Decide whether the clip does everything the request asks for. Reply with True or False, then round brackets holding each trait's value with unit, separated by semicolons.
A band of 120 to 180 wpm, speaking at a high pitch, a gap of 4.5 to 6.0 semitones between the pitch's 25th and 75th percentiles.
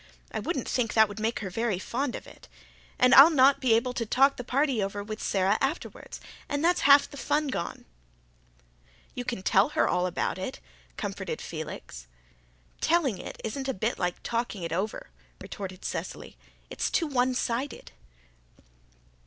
True (165 wpm; 235 Hz; 5.1 semitones)